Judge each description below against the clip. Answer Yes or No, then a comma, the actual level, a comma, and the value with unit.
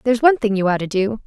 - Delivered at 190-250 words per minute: No, fast, 330 wpm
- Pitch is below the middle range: No, high, 220 Hz